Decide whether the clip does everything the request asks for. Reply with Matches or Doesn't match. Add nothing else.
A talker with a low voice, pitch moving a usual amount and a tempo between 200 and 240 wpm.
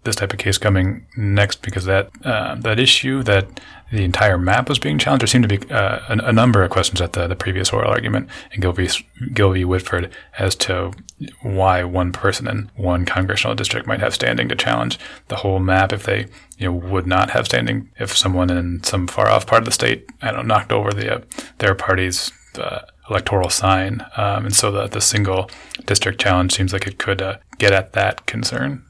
Matches